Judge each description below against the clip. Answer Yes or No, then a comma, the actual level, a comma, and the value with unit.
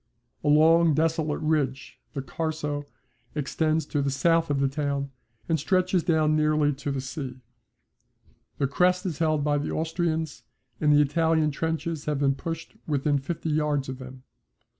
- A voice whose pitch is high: No, medium, 150 Hz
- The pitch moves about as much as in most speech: No, narrow, 2.3 semitones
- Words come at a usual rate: Yes, average, 160 wpm